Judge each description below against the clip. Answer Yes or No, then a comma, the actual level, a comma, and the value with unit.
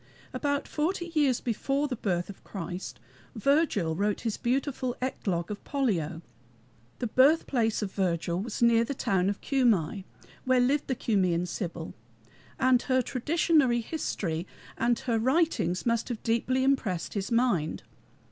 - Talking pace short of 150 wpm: Yes, average, 140 wpm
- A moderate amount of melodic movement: No, wide, 5.8 semitones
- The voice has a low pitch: No, high, 235 Hz